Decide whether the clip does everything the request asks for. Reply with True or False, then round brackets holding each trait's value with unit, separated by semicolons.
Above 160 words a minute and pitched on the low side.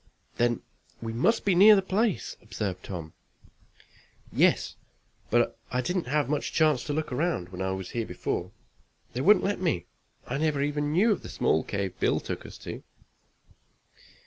False (170 wpm; 145 Hz)